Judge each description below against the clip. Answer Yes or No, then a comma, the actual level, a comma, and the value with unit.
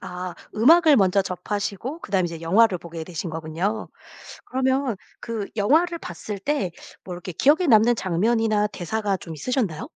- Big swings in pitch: No, average, 5.0 semitones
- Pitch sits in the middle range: No, high, 205 Hz